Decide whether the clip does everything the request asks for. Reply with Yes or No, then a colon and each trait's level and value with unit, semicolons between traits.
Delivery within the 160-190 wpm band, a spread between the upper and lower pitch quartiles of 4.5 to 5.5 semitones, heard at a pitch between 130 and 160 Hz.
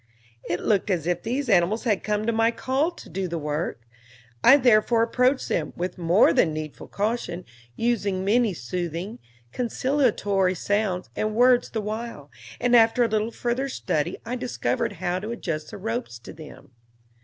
No: average, 165 wpm; average, 5.1 semitones; high, 210 Hz